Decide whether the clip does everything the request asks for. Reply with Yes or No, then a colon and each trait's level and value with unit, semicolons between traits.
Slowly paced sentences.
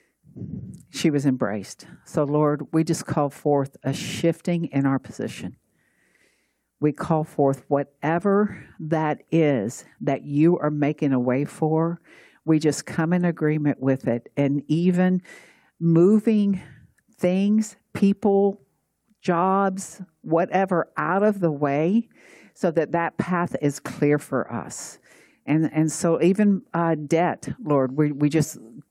Yes: slow, 130 wpm